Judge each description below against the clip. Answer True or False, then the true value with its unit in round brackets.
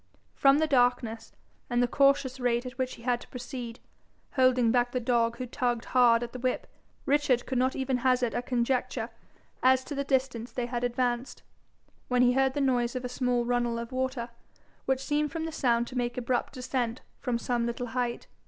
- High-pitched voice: True (250 Hz)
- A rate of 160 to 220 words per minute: True (200 wpm)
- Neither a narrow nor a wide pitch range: False (1.4 semitones)